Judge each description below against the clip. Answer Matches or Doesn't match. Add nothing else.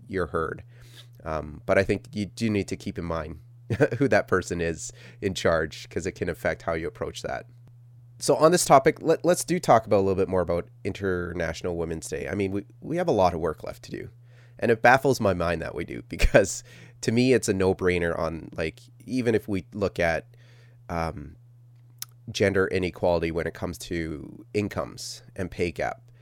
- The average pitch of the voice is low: Matches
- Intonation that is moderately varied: Doesn't match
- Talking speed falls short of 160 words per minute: Doesn't match